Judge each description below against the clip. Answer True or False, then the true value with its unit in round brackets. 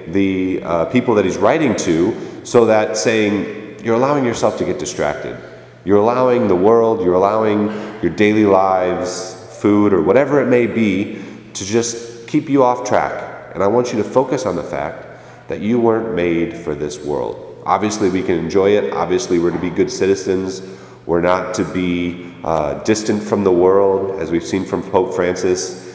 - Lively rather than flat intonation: False (3.7 semitones)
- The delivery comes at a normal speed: True (185 wpm)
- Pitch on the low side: True (100 Hz)